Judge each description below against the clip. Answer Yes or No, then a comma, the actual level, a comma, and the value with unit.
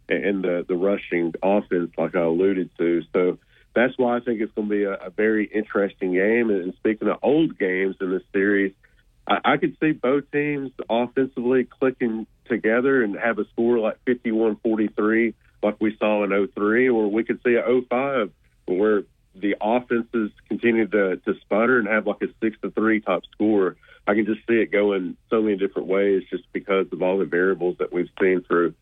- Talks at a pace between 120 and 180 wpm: No, average, 195 wpm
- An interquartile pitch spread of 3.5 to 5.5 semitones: No, average, 3.0 semitones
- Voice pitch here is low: Yes, low, 105 Hz